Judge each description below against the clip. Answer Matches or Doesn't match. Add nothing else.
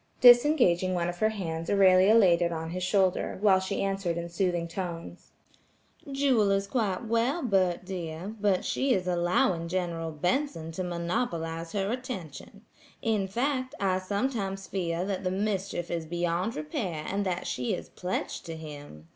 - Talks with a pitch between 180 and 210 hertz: Matches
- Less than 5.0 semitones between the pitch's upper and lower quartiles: Matches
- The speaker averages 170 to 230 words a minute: Doesn't match